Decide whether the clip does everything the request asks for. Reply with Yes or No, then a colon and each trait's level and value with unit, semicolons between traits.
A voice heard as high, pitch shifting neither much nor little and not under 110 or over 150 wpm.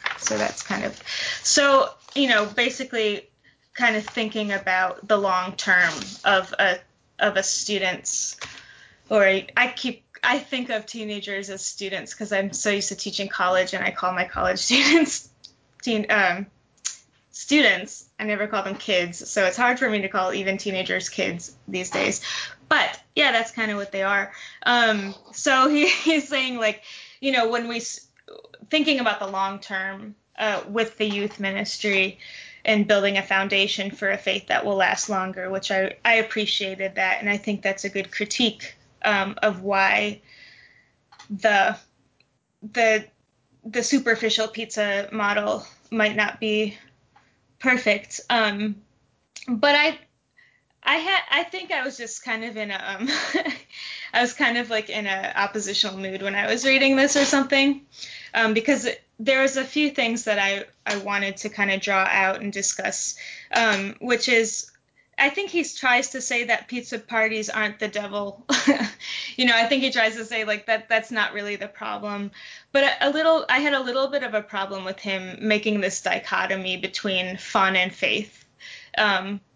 No: high, 215 Hz; average, 3.8 semitones; average, 170 wpm